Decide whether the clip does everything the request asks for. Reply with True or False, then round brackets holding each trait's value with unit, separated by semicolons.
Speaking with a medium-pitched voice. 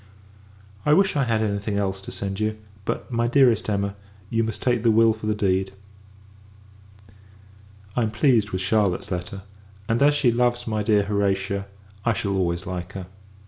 False (105 Hz)